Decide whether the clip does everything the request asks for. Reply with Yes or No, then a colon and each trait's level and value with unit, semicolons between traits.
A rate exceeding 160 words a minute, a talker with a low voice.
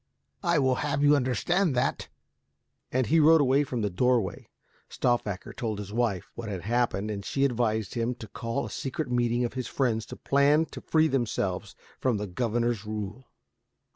Yes: average, 170 wpm; low, 120 Hz